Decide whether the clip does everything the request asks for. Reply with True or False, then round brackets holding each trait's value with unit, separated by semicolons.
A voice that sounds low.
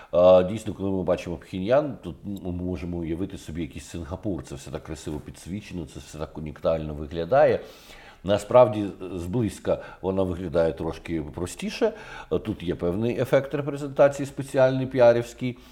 True (90 Hz)